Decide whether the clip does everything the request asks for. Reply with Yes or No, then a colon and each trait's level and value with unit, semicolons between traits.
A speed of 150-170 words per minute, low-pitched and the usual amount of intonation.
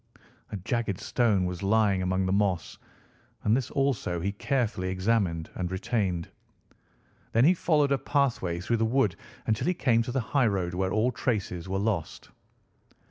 Yes: average, 160 wpm; low, 105 Hz; average, 4.6 semitones